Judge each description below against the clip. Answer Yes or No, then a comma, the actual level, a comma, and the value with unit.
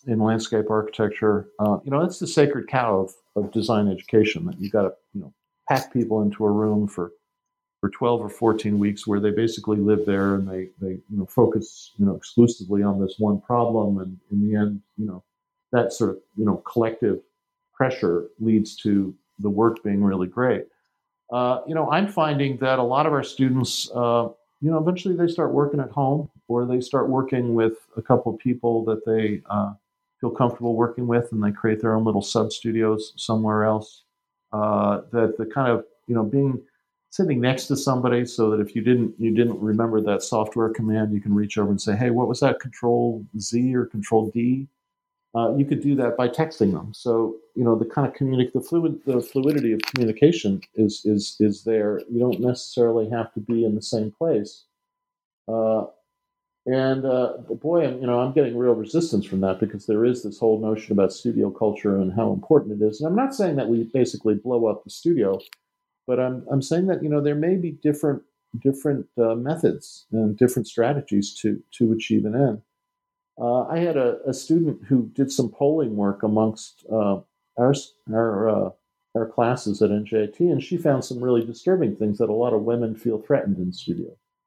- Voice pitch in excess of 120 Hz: No, low, 115 Hz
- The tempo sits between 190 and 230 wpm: Yes, average, 200 wpm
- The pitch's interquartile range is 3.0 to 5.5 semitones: Yes, average, 4.5 semitones